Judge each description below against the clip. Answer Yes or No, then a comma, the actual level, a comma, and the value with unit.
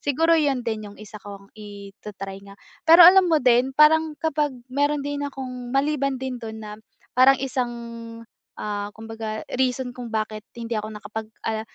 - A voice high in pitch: Yes, high, 245 Hz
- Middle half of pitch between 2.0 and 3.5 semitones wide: No, average, 4.6 semitones